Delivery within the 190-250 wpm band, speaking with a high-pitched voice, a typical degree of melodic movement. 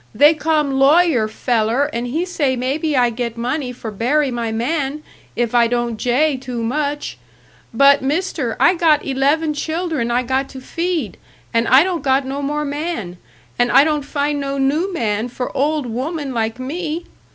No: average, 175 wpm; very high, 275 Hz; average, 4.0 semitones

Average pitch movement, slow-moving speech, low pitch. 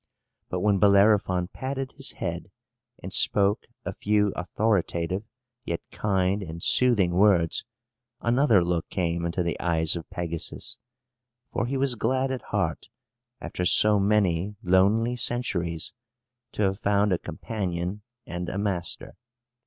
Yes: average, 3.4 semitones; slow, 130 wpm; very low, 95 Hz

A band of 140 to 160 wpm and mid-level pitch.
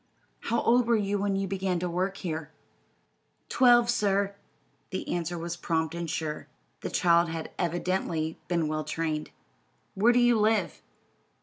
Yes: average, 150 wpm; medium, 180 Hz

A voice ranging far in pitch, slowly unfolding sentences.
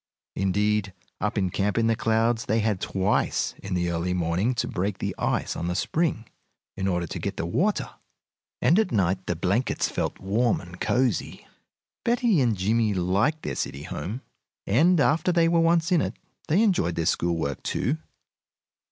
No: wide, 8.0 semitones; average, 180 wpm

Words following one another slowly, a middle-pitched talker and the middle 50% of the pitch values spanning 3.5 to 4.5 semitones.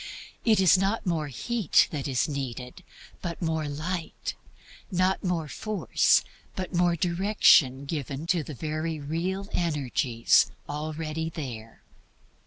Yes: slow, 130 wpm; medium, 160 Hz; average, 4.0 semitones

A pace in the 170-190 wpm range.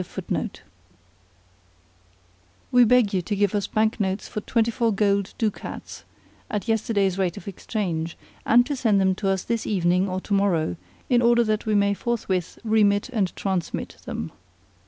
No: average, 155 wpm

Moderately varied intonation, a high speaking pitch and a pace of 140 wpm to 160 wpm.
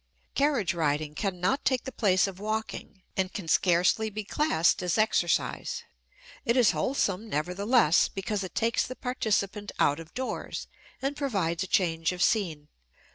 Yes: average, 4.6 semitones; high, 195 Hz; average, 150 wpm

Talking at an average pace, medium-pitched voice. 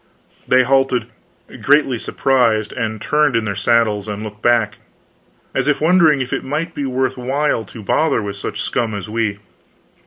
No: average, 165 wpm; low, 120 Hz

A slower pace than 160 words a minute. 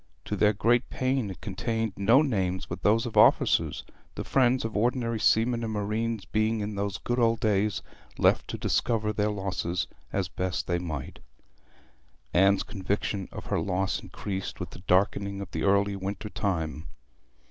No: average, 165 wpm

